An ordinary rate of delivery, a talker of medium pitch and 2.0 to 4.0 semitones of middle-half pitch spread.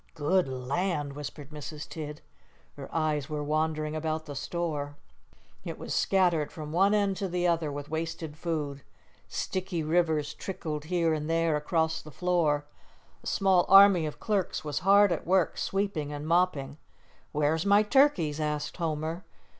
Yes: average, 155 wpm; medium, 160 Hz; average, 3.1 semitones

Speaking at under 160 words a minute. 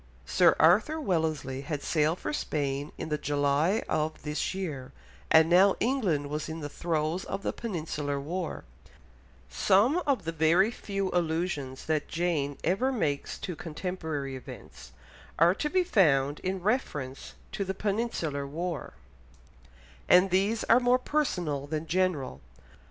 Yes: average, 140 wpm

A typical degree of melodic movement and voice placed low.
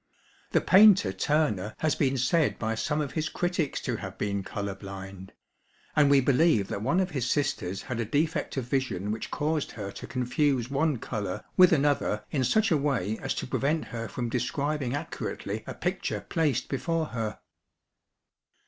No: wide, 6.0 semitones; low, 130 Hz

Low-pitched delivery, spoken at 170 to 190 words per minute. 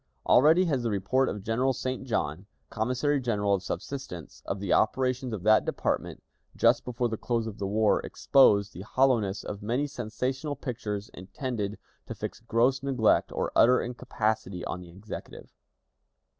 No: low, 115 Hz; average, 155 wpm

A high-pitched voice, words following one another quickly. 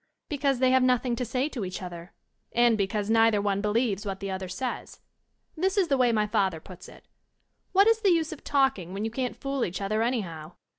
Yes: high, 225 Hz; fast, 225 wpm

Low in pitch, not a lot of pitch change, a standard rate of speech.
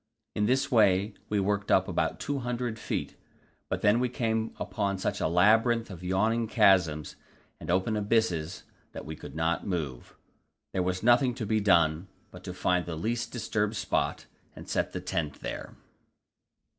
No: low, 100 Hz; average, 4.1 semitones; average, 165 wpm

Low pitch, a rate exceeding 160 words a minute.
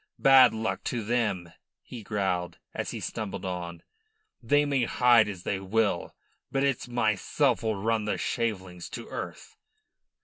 No: low, 110 Hz; average, 145 wpm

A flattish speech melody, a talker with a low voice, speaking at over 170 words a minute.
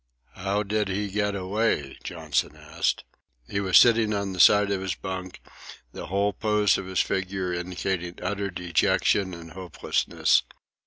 No: narrow, 2.0 semitones; very low, 95 Hz; average, 150 wpm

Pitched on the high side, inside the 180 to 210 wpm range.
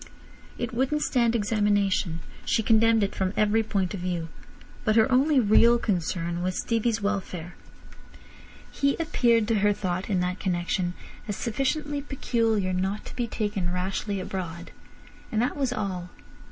No: high, 210 Hz; average, 150 wpm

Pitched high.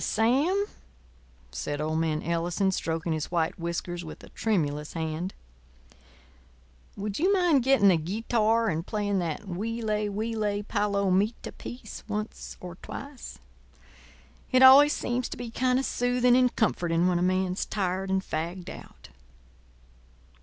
Yes: high, 200 Hz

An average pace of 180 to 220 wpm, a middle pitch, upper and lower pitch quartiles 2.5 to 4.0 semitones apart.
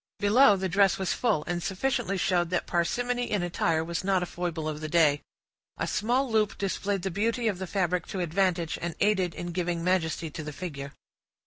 Yes: average, 200 wpm; medium, 180 Hz; average, 3.1 semitones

